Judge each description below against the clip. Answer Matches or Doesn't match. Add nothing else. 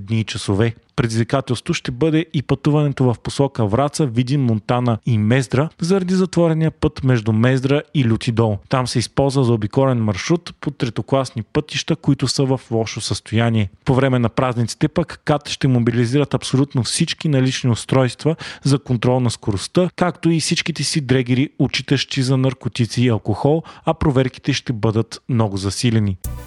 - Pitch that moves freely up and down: Doesn't match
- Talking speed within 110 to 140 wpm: Doesn't match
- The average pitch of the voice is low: Matches